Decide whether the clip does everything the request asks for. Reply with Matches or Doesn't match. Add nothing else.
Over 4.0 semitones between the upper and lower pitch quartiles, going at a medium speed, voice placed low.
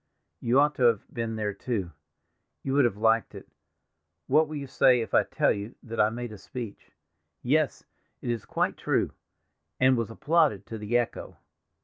Doesn't match